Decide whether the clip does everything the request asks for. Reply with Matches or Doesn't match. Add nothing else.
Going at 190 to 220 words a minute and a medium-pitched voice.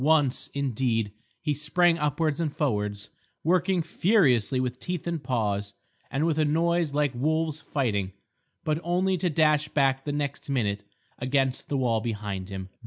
Doesn't match